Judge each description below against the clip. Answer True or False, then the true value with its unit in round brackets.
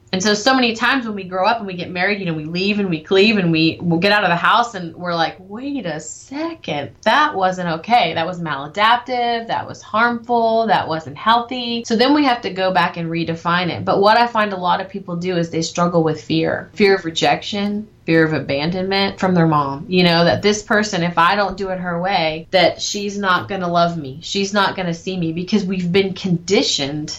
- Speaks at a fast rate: True (240 wpm)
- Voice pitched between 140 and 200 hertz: True (185 Hz)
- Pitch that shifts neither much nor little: True (3.9 semitones)